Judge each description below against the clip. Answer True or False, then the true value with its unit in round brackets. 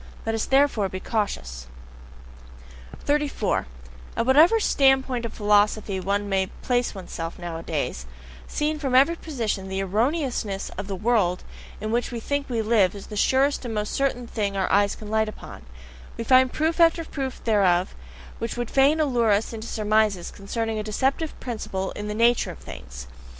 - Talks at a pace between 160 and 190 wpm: True (165 wpm)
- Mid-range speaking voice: False (220 Hz)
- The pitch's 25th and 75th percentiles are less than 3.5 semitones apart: False (4.8 semitones)